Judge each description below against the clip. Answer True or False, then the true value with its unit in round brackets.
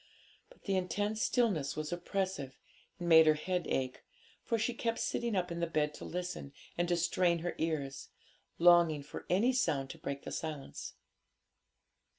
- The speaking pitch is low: False (175 Hz)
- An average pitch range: True (3.8 semitones)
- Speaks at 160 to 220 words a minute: True (165 wpm)